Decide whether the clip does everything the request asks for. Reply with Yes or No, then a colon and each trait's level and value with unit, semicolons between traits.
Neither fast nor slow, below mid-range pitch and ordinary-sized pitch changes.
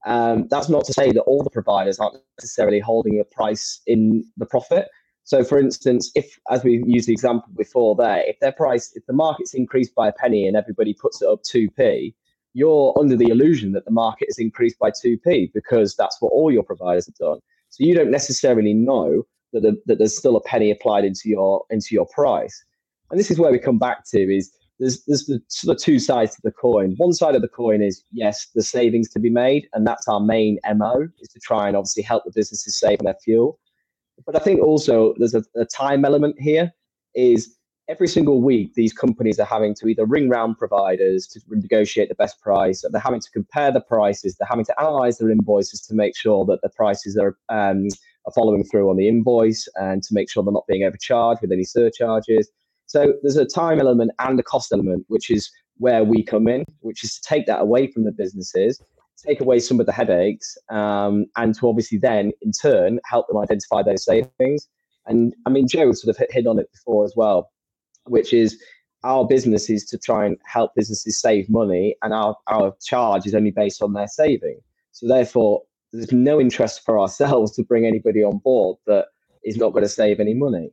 No: fast, 215 wpm; low, 115 Hz; average, 3.7 semitones